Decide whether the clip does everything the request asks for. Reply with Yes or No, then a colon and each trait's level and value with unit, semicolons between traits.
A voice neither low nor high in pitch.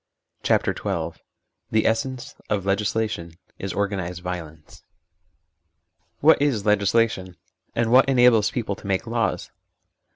No: low, 105 Hz